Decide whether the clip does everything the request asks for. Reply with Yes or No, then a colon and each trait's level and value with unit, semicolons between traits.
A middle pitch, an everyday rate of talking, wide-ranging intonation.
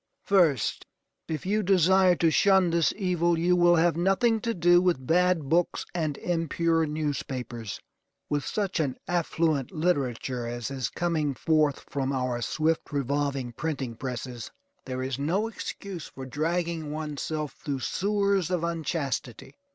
No: medium, 160 Hz; average, 145 wpm; average, 4.4 semitones